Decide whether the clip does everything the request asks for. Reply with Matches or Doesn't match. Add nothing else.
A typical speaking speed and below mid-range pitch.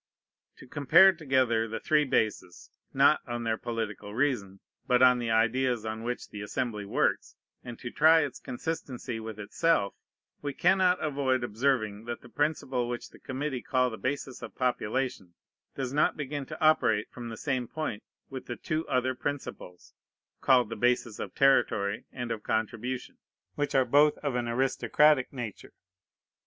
Matches